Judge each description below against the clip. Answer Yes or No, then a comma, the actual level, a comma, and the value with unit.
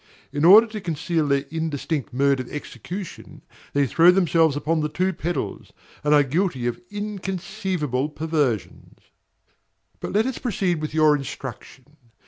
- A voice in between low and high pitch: Yes, medium, 160 Hz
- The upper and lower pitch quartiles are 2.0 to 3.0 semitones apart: No, average, 4.4 semitones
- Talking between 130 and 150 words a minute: Yes, average, 140 wpm